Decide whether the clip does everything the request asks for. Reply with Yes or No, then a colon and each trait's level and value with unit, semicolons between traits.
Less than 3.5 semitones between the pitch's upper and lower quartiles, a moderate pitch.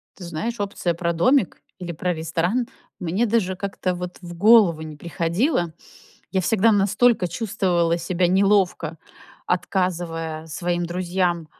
Yes: average, 2.7 semitones; medium, 180 Hz